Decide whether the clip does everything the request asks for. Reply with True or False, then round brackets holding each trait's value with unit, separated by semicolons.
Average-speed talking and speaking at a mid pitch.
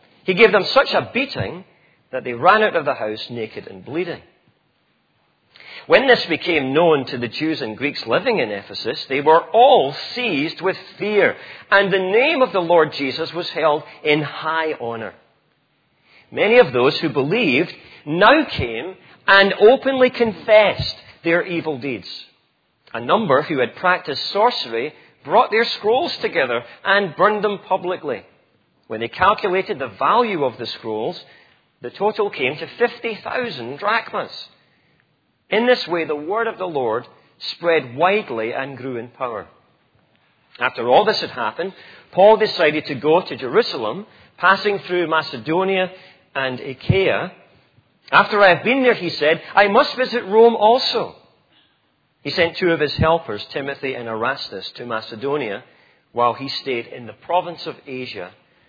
True (150 wpm; 175 Hz)